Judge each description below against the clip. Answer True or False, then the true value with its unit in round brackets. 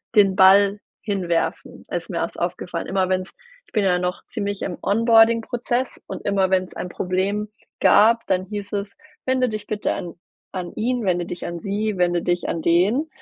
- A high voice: True (200 Hz)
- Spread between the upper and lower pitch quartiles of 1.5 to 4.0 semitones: True (2.9 semitones)